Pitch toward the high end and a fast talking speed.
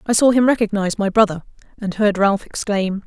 No: high, 205 Hz; average, 195 wpm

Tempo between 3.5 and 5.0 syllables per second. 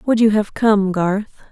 Yes: 4.0 syllables/s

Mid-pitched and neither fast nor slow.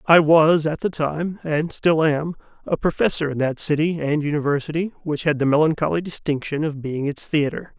Yes: medium, 155 Hz; average, 185 wpm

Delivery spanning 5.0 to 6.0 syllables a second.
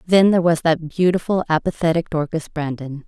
Yes: 5.5 syllables/s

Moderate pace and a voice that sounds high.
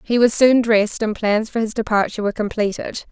No: fast, 210 wpm; high, 220 Hz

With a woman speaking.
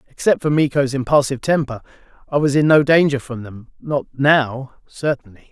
No: male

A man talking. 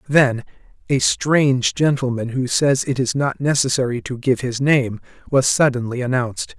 Yes: male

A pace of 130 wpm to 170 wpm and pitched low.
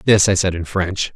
No: fast, 260 wpm; very low, 95 Hz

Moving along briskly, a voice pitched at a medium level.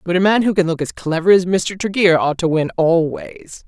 Yes: fast, 245 wpm; medium, 175 Hz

